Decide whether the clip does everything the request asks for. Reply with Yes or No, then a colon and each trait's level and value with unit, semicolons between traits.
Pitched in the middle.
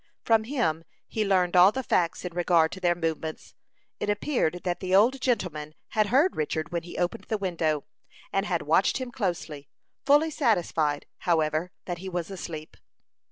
Yes: medium, 180 Hz